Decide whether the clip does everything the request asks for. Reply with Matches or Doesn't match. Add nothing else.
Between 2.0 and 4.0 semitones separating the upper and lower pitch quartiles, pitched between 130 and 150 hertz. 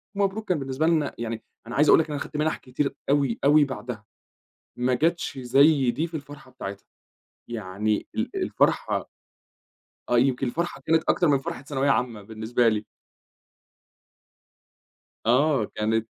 Doesn't match